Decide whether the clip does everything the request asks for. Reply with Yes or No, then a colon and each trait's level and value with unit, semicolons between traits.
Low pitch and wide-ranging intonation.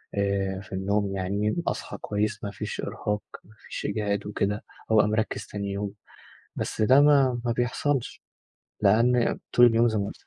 No: low, 105 Hz; narrow, 2.6 semitones